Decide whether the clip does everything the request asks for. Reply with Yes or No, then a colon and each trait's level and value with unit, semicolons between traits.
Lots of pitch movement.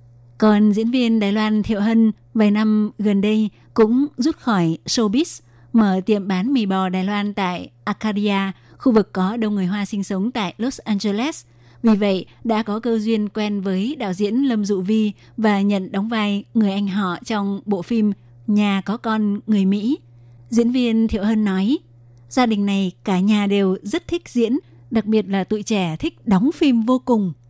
No: narrow, 2.4 semitones